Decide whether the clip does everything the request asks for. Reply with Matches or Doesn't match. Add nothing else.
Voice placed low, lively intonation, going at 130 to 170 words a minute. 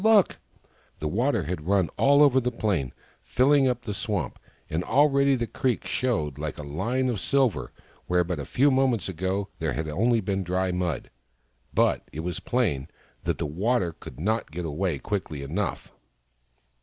Doesn't match